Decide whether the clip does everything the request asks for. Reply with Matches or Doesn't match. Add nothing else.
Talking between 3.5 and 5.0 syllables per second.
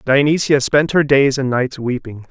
Matches